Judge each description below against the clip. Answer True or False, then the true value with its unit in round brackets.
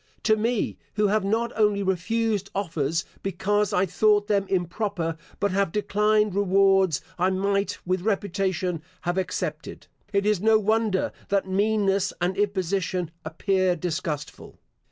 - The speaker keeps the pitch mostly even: True (2.3 semitones)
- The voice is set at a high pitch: True (195 Hz)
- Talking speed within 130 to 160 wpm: True (135 wpm)